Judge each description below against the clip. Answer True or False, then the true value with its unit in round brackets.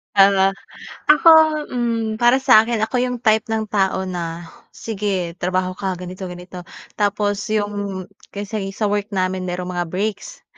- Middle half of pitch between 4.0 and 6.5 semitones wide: False (3.0 semitones)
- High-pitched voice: True (200 Hz)